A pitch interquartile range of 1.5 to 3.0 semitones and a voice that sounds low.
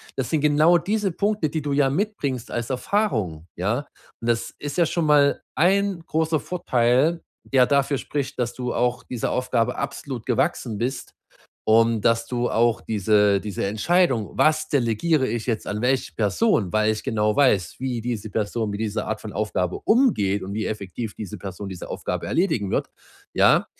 No: wide, 5.7 semitones; low, 120 Hz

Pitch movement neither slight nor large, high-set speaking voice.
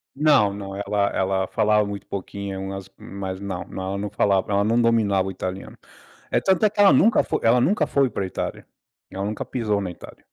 No: average, 3.0 semitones; low, 100 Hz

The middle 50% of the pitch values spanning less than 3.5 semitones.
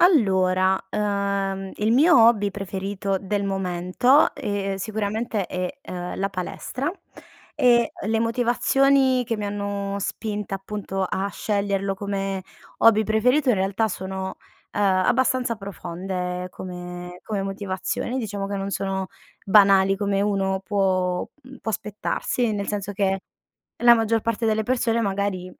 Yes: narrow, 2.4 semitones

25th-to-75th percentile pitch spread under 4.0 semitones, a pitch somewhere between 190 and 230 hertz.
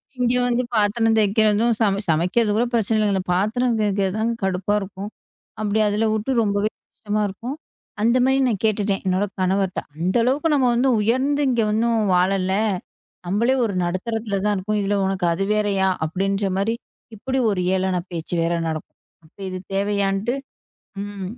Yes: average, 2.9 semitones; high, 205 Hz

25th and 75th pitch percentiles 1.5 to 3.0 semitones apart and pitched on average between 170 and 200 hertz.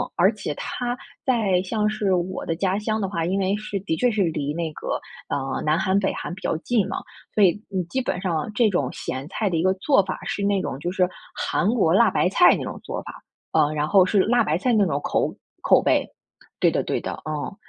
No: average, 4.2 semitones; high, 190 Hz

